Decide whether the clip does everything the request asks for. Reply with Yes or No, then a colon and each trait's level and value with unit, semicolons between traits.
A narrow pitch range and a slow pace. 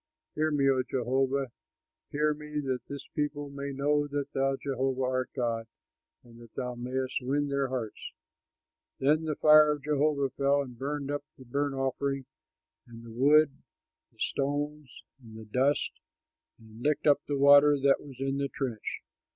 No: narrow, 2.1 semitones; average, 165 wpm